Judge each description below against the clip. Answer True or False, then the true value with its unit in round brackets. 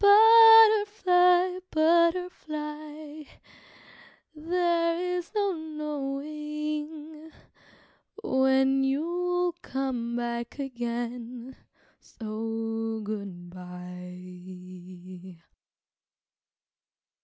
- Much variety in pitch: True (7.2 semitones)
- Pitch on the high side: True (295 Hz)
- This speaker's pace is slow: True (50 wpm)